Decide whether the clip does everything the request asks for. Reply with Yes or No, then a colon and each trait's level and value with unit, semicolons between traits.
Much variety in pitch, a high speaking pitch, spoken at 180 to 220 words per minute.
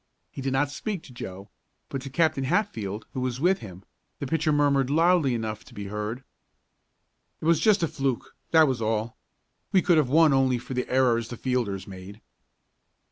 No: wide, 5.7 semitones; low, 130 Hz; average, 190 wpm